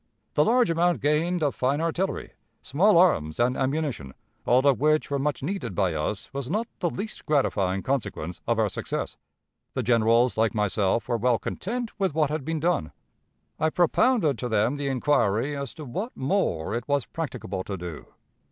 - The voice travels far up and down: Yes, wide, 6.3 semitones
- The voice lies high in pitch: No, low, 135 Hz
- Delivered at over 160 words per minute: Yes, average, 180 wpm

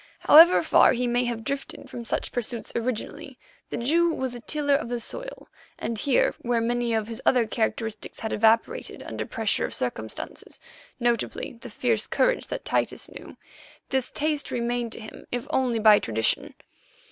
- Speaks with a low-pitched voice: No, high, 240 Hz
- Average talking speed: Yes, average, 160 wpm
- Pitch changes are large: No, narrow, 2.6 semitones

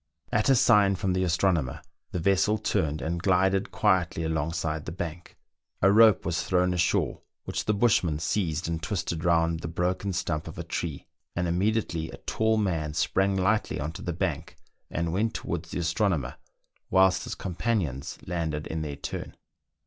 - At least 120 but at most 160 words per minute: No, average, 170 wpm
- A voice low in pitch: Yes, very low, 90 Hz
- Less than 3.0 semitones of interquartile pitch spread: No, average, 3.3 semitones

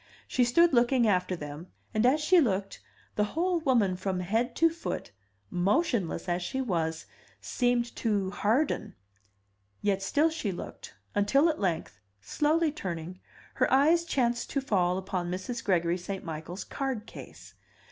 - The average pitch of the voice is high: Yes, high, 210 Hz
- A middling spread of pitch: No, wide, 6.8 semitones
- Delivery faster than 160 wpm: No, average, 145 wpm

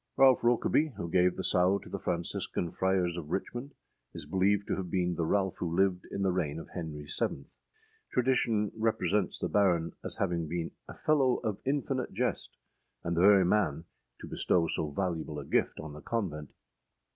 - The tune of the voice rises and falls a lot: No, average, 3.7 semitones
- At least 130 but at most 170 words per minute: No, average, 180 wpm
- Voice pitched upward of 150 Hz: No, very low, 95 Hz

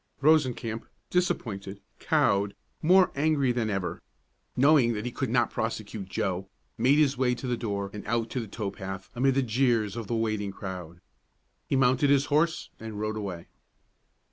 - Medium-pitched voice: No, low, 115 Hz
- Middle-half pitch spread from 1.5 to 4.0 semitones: No, average, 4.8 semitones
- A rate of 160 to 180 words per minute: Yes, average, 170 wpm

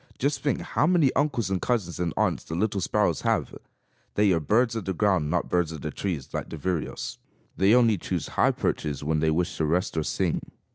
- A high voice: No, very low, 90 Hz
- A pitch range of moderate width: No, wide, 5.8 semitones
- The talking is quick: Yes, fast, 220 wpm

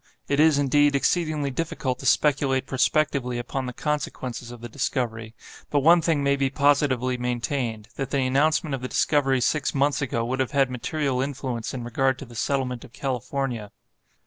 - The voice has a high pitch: No, low, 135 Hz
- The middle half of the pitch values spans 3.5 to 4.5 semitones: No, narrow, 2.5 semitones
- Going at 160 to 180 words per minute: Yes, average, 170 wpm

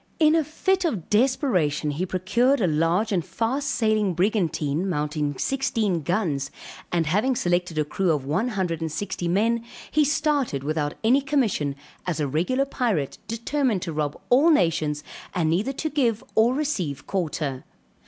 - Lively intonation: Yes, wide, 8.3 semitones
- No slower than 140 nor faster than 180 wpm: Yes, average, 160 wpm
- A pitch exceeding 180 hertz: Yes, high, 190 Hz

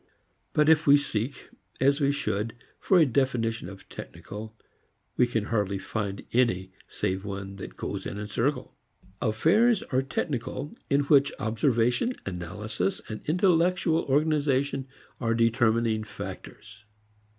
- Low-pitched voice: Yes, low, 120 Hz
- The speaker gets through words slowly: Yes, slow, 130 wpm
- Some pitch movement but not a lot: Yes, average, 5.0 semitones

